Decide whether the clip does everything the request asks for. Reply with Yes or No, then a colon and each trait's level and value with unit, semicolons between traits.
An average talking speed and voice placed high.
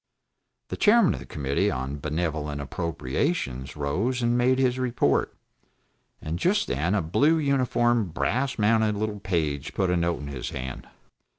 No: average, 155 wpm; very low, 90 Hz